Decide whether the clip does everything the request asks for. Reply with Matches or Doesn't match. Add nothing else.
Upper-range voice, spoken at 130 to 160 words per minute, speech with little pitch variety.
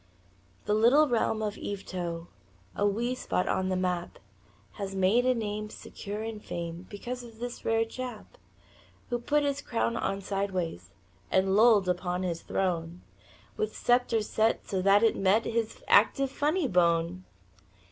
Doesn't match